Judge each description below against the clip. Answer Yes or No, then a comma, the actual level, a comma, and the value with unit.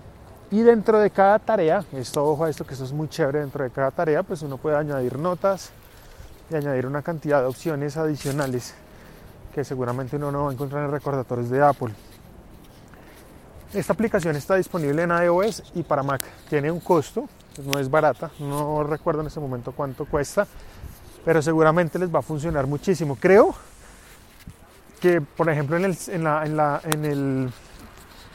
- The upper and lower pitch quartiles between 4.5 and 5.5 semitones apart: No, average, 3.8 semitones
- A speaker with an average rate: Yes, average, 175 wpm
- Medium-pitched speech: Yes, medium, 150 Hz